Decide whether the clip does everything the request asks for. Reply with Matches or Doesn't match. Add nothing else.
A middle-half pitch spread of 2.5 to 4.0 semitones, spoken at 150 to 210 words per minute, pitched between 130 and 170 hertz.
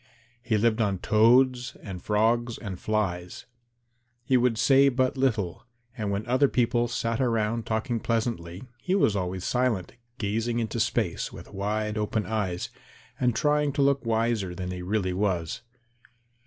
Doesn't match